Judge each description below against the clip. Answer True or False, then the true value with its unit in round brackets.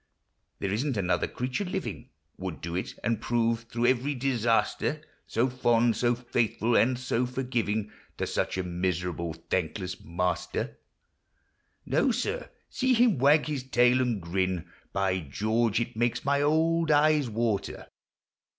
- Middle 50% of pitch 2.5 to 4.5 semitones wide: False (5.3 semitones)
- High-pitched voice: False (120 Hz)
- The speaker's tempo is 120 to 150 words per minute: True (140 wpm)